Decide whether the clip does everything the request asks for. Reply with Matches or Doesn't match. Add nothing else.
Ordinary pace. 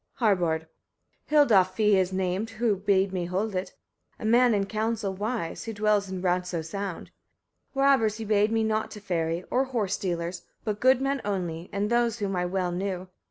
Matches